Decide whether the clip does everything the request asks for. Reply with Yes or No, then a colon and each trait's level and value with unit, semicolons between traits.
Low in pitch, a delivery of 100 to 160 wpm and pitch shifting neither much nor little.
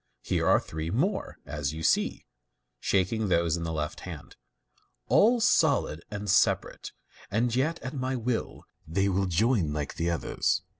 No: very low, 95 Hz; average, 155 wpm; wide, 7.6 semitones